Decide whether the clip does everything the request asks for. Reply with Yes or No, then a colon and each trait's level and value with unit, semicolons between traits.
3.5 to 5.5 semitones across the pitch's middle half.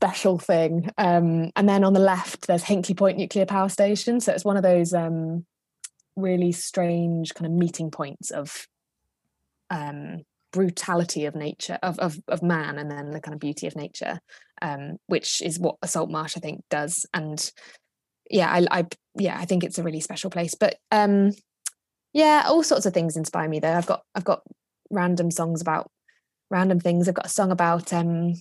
No: average, 2.9 semitones